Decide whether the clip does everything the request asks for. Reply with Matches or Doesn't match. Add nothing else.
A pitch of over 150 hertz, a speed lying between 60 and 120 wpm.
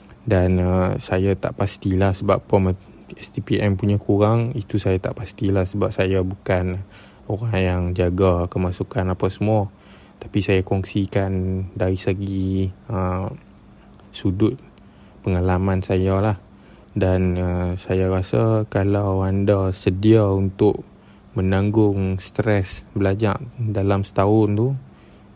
Doesn't match